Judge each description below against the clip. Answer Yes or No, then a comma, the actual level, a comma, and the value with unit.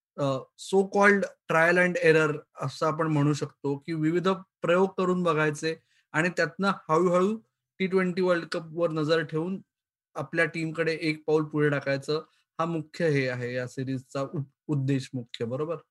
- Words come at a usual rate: No, fast, 150 wpm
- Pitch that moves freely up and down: No, average, 3.8 semitones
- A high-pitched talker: No, medium, 160 Hz